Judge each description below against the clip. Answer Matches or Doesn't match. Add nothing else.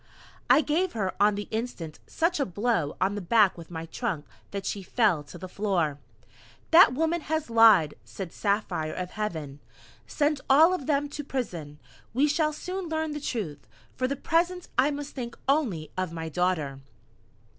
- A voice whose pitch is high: Matches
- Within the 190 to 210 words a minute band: Doesn't match